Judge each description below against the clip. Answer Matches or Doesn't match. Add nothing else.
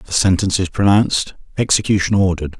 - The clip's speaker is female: Doesn't match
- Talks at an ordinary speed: Doesn't match